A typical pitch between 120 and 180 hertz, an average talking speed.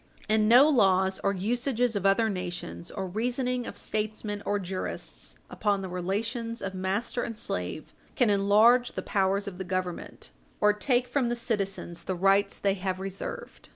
No: high, 200 Hz; average, 165 wpm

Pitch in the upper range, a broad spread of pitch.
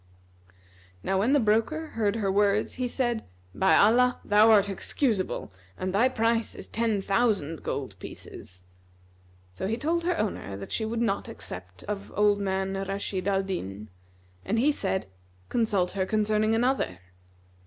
No: high, 205 Hz; average, 3.3 semitones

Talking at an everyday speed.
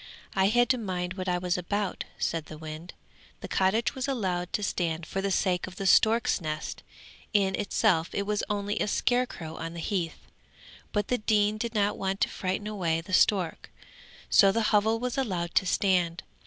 Yes: average, 190 wpm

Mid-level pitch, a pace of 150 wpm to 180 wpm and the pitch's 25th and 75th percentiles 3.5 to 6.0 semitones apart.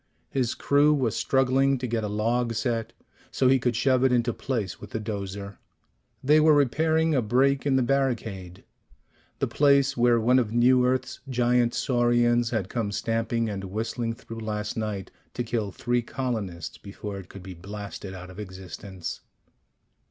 No: low, 120 Hz; average, 165 wpm; average, 3.8 semitones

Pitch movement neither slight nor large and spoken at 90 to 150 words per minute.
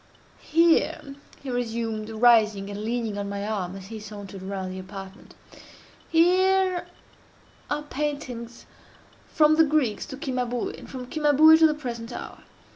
No: wide, 6.4 semitones; average, 140 wpm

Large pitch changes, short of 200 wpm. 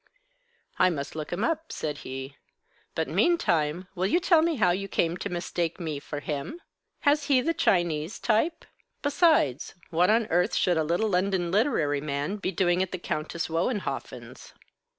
Yes: wide, 6.0 semitones; average, 170 wpm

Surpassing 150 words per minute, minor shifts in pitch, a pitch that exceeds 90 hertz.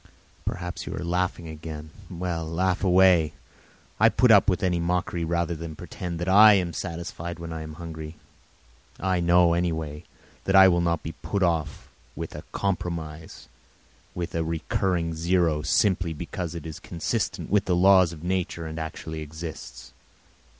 No: average, 160 wpm; narrow, 2.0 semitones; very low, 85 Hz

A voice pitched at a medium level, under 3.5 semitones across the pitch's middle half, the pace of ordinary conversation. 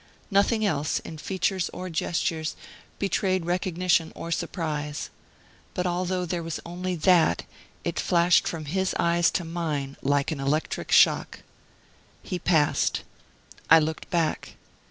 No: medium, 170 Hz; narrow, 2.5 semitones; slow, 130 wpm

